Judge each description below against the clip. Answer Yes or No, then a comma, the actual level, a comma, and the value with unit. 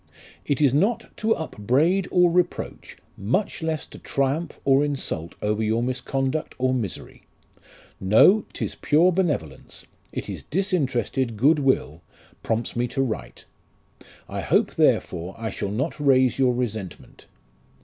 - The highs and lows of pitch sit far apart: Yes, wide, 6.2 semitones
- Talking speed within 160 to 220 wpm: No, slow, 135 wpm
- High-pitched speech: No, low, 135 Hz